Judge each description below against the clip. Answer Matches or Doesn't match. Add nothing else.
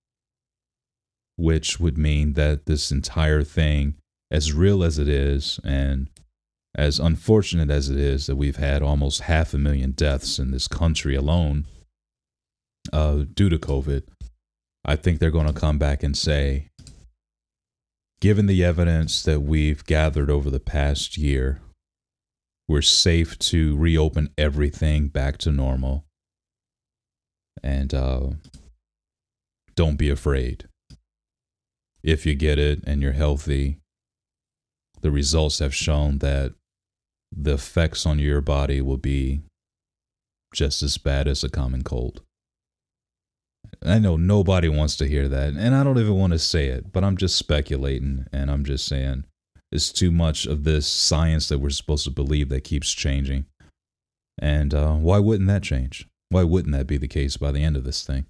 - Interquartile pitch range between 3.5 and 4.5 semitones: Doesn't match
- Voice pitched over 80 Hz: Doesn't match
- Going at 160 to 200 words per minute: Doesn't match